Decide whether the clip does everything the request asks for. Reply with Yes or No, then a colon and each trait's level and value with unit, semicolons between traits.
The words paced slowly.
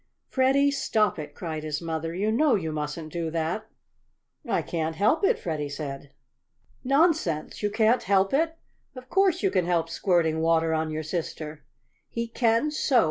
No: average, 165 wpm